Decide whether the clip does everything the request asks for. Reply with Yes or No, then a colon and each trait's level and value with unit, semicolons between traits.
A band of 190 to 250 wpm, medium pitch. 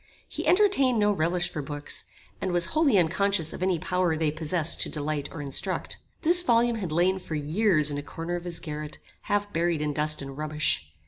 Yes: average, 200 wpm; medium, 170 Hz